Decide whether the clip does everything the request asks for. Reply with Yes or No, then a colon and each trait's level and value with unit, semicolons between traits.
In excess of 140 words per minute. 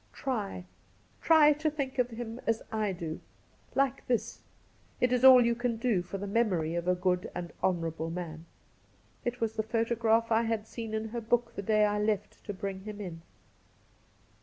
Yes: average, 190 wpm